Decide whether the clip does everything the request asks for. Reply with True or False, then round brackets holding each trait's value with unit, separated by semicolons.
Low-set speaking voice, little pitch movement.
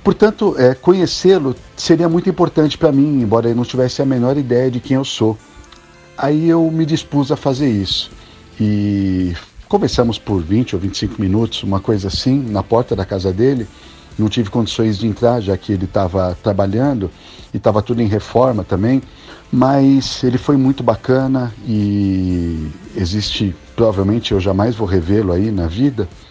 False (115 Hz; 5.3 semitones)